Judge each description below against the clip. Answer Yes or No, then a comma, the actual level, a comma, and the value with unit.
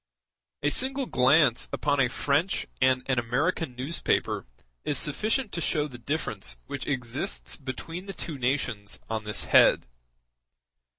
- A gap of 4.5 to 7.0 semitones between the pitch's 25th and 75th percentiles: Yes, average, 4.9 semitones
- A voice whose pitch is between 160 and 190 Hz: No, medium, 140 Hz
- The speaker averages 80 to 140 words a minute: Yes, slow, 135 wpm